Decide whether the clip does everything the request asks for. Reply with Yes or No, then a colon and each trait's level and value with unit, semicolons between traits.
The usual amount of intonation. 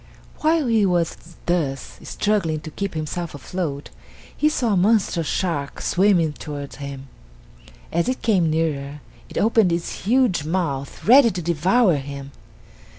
No: wide, 5.8 semitones